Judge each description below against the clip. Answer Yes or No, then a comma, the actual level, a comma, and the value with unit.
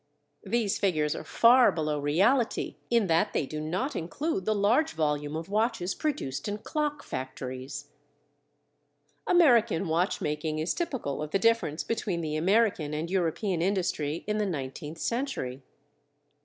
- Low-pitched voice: No, medium, 180 Hz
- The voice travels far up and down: Yes, wide, 7.2 semitones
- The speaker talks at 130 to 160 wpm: Yes, average, 140 wpm